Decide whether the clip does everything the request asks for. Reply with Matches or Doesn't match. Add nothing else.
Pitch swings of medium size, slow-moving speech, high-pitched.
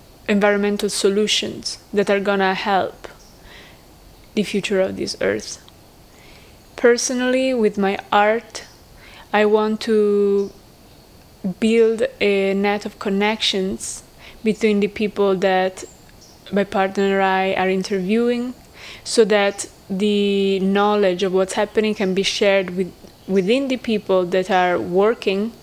Doesn't match